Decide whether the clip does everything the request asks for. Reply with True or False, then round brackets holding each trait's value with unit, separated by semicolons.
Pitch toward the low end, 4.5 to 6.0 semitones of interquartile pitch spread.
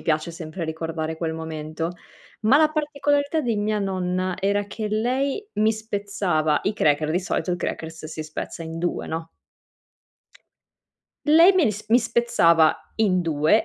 False (185 Hz; 5.6 semitones)